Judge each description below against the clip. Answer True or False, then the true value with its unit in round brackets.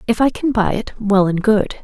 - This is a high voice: True (215 Hz)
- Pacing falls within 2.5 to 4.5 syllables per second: False (5.1 syllables/s)